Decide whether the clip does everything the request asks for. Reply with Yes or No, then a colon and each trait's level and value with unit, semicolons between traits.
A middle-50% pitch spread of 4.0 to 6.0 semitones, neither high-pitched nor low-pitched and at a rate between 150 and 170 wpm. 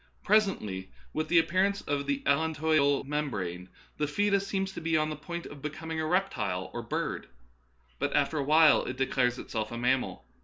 No: average, 4.3 semitones; medium, 150 Hz; average, 185 wpm